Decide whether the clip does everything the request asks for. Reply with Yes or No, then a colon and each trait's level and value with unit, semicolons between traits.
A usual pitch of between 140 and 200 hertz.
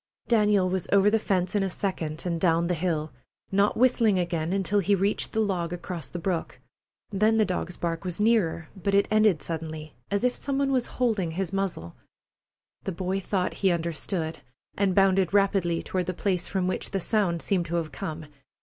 Yes: medium, 185 Hz